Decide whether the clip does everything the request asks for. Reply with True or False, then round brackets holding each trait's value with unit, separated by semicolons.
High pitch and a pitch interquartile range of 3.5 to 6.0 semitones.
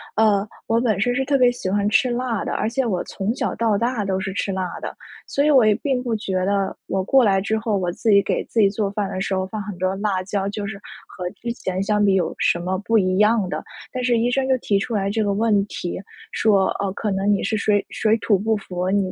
False (205 Hz; 2.9 semitones)